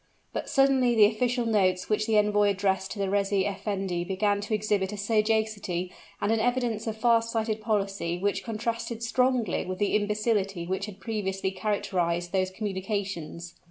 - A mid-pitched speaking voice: No, high, 205 Hz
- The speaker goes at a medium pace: Yes, average, 160 wpm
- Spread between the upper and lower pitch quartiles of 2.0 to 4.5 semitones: Yes, narrow, 2.6 semitones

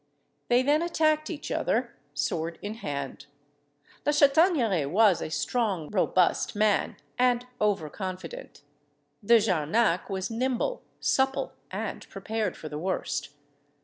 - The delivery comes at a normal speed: No, slow, 120 wpm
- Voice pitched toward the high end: Yes, high, 210 Hz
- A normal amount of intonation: No, wide, 7.0 semitones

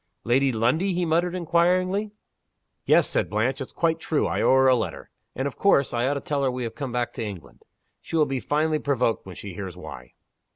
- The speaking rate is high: Yes, fast, 220 wpm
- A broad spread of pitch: Yes, wide, 5.7 semitones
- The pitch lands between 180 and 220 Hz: No, low, 135 Hz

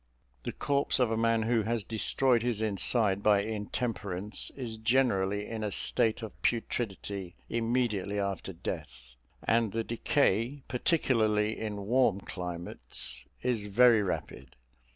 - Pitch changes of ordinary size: Yes, average, 3.0 semitones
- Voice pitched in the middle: No, low, 110 Hz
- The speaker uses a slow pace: Yes, slow, 130 wpm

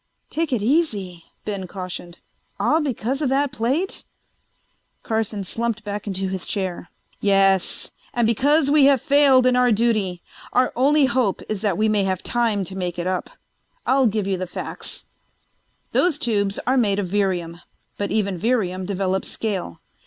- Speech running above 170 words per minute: No, average, 160 wpm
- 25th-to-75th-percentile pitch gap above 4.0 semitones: Yes, average, 5.0 semitones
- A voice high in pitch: Yes, high, 210 Hz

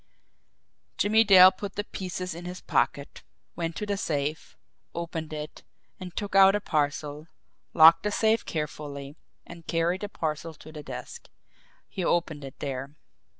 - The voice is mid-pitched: Yes, medium, 165 Hz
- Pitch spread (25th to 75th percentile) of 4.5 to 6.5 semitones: No, average, 4.1 semitones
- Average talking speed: Yes, average, 150 wpm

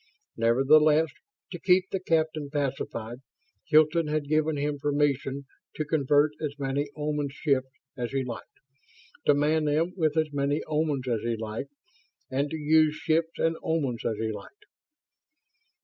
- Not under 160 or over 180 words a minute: No, average, 150 wpm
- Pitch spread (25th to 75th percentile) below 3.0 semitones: Yes, narrow, 2.4 semitones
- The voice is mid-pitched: Yes, medium, 150 Hz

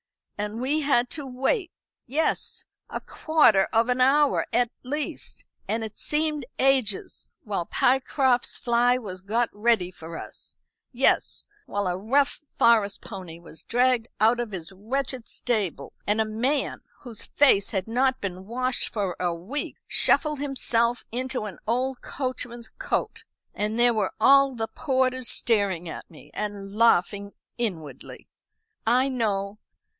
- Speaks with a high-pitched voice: Yes, high, 235 Hz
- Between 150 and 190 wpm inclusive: No, average, 140 wpm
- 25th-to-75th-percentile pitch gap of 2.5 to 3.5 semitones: No, average, 4.3 semitones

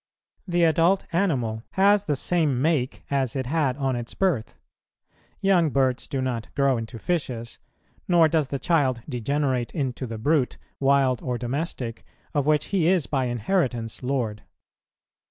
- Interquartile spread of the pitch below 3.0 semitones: No, average, 4.8 semitones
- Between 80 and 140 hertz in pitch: Yes, low, 135 Hz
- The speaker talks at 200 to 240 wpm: No, average, 150 wpm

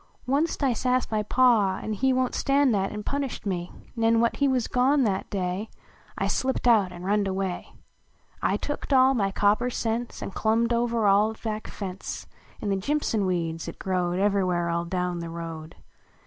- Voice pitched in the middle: No, high, 210 Hz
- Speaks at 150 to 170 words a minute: No, average, 190 wpm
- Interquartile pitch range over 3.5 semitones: Yes, average, 4.8 semitones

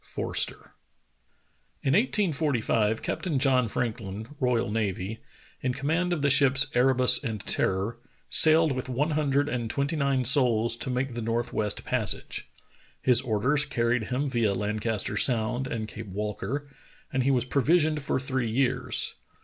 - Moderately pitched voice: No, low, 125 Hz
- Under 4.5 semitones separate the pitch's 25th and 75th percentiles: Yes, average, 3.7 semitones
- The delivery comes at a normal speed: Yes, average, 150 wpm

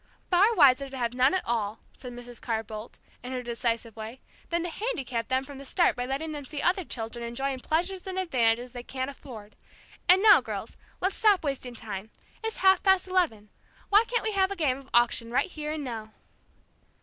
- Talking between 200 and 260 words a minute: Yes, fast, 205 wpm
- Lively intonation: Yes, wide, 7.1 semitones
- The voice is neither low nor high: No, very high, 265 Hz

